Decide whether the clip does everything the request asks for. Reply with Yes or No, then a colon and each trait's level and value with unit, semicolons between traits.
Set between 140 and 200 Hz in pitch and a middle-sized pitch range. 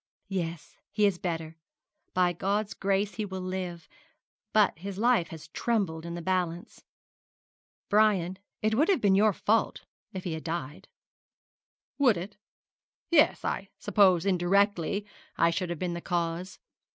Yes: medium, 185 Hz; average, 3.2 semitones